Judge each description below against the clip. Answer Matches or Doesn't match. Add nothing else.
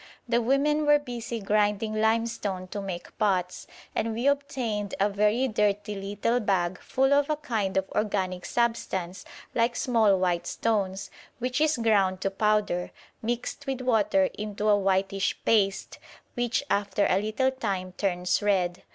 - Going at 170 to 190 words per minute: Doesn't match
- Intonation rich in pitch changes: Doesn't match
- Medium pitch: Doesn't match